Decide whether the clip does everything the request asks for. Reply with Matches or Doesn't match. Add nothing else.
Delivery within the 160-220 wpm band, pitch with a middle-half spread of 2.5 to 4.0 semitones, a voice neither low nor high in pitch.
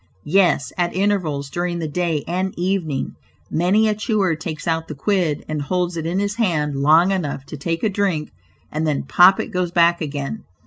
Matches